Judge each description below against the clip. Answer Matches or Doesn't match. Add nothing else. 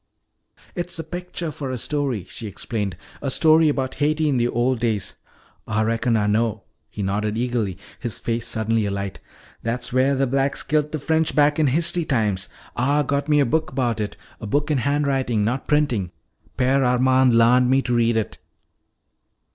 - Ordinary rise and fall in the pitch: Matches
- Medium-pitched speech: Doesn't match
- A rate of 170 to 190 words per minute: Matches